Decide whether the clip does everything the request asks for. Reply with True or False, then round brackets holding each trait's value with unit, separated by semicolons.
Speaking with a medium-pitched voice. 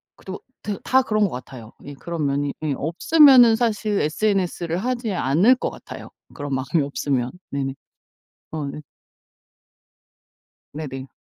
True (160 Hz)